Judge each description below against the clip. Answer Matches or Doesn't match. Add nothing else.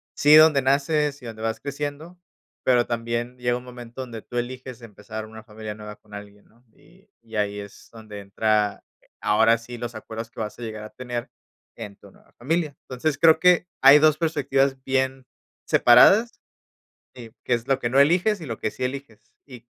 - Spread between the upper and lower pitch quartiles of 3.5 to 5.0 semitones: Matches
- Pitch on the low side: Matches